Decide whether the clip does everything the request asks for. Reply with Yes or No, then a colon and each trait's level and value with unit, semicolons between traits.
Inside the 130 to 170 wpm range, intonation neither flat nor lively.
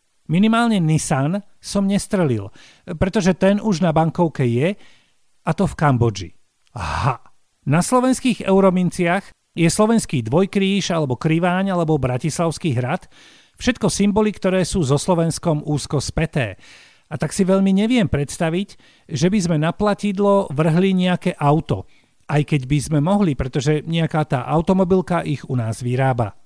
Yes: average, 140 wpm; average, 4.7 semitones